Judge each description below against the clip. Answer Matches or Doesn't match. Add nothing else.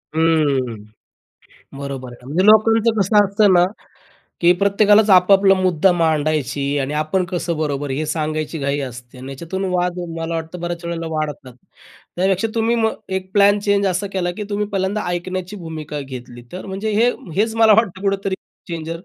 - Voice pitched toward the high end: Doesn't match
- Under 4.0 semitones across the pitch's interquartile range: Doesn't match